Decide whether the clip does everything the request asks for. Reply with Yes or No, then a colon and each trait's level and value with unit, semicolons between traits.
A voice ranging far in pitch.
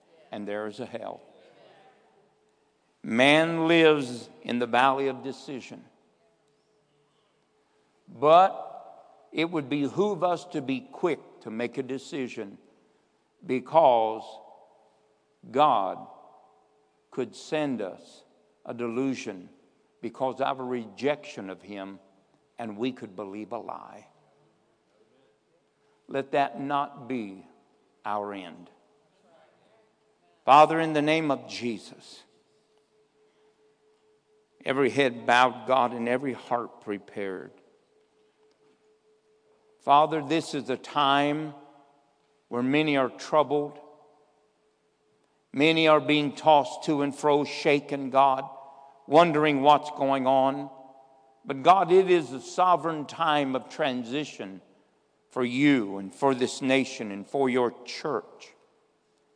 No: average, 3.8 semitones